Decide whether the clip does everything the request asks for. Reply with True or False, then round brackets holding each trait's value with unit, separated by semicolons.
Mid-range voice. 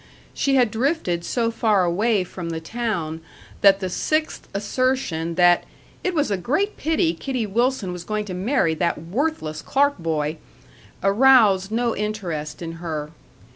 False (200 Hz)